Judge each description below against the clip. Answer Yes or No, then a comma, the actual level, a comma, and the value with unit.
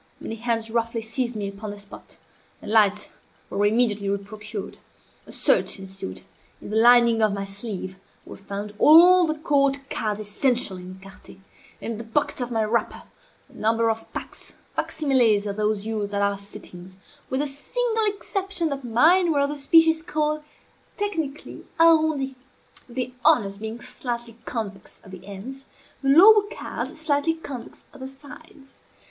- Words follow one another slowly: No, average, 165 wpm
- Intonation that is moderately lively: No, wide, 6.0 semitones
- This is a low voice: No, high, 235 Hz